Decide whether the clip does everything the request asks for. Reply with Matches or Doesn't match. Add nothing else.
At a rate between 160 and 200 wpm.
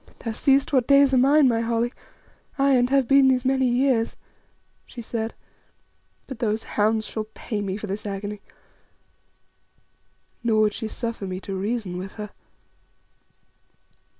Doesn't match